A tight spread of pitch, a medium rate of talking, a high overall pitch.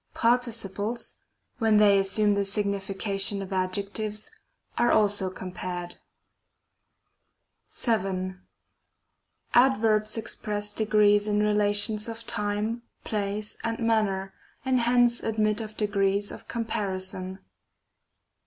No: narrow, 2.0 semitones; slow, 95 wpm; high, 210 Hz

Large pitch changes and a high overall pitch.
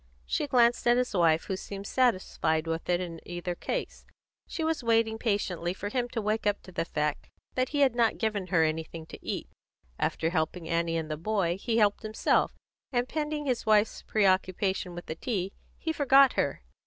Yes: wide, 5.9 semitones; high, 200 Hz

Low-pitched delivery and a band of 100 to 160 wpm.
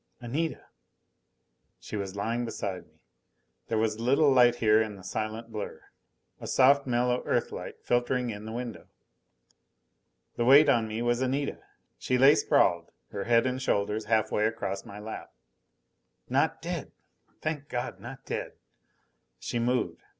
Yes: low, 120 Hz; average, 150 wpm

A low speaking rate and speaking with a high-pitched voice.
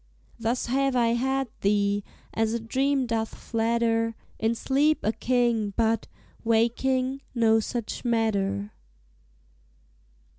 Yes: slow, 110 wpm; high, 230 Hz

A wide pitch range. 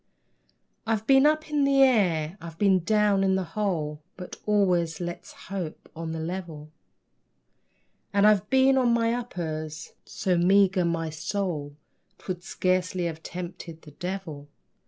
No: average, 4.2 semitones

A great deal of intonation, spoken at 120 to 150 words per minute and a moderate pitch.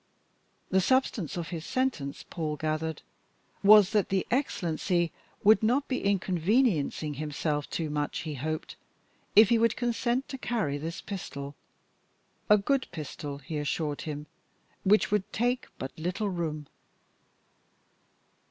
Yes: wide, 6.1 semitones; slow, 135 wpm; medium, 175 Hz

